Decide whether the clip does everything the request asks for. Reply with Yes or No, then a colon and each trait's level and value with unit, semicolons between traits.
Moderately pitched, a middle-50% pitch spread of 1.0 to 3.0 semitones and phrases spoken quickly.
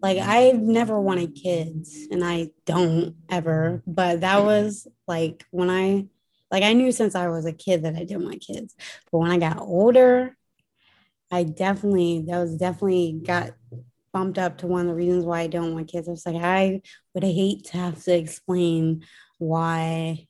No: medium, 175 Hz; narrow, 2.4 semitones; average, 185 wpm